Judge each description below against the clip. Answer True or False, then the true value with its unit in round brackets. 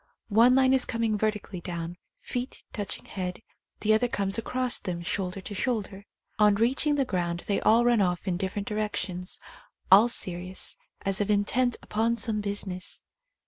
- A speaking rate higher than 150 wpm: True (170 wpm)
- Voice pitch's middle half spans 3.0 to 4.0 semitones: True (3.7 semitones)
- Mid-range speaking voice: False (205 Hz)